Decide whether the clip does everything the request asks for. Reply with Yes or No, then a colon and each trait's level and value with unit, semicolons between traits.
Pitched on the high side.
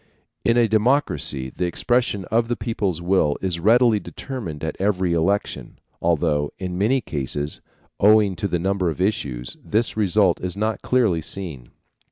No: very low, 95 Hz